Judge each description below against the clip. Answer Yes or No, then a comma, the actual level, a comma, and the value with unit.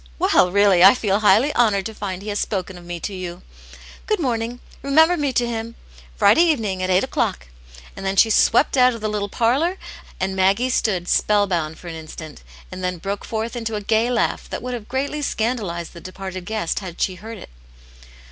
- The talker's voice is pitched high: Yes, high, 210 Hz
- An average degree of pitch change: Yes, average, 4.3 semitones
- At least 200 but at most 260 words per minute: Yes, fast, 205 wpm